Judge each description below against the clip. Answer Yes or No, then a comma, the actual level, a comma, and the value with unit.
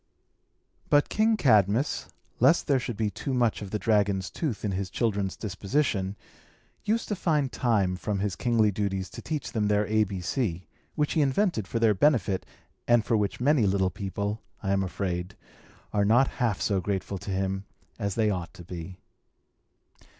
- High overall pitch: No, low, 105 Hz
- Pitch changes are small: No, average, 4.1 semitones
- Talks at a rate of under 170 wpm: No, average, 175 wpm